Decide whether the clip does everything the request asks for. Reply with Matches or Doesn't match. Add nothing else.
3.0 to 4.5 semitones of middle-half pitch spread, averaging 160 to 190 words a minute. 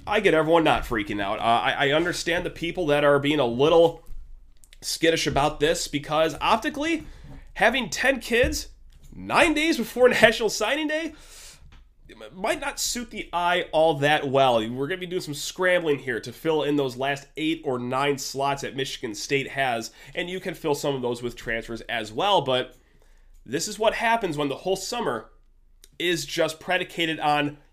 Doesn't match